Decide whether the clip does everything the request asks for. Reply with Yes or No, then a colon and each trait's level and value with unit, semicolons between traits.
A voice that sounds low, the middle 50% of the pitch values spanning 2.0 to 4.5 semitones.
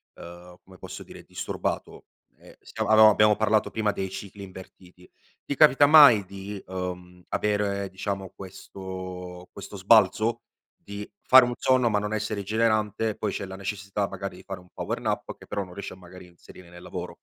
Yes: low, 100 Hz; narrow, 2.5 semitones